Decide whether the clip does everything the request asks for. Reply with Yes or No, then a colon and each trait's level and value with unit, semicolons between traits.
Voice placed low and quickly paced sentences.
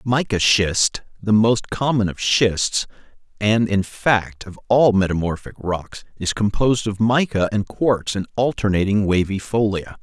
No: low, 105 Hz; average, 145 wpm